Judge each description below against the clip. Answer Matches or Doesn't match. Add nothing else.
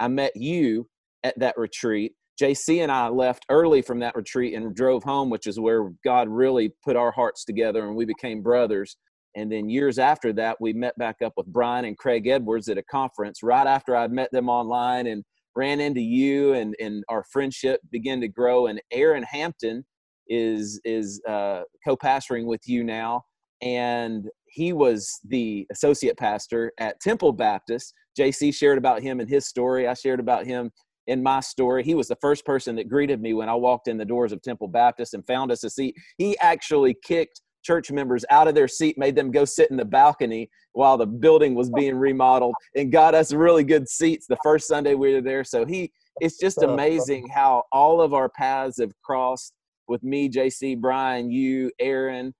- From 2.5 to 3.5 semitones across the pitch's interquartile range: Matches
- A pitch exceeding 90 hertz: Matches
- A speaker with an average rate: Matches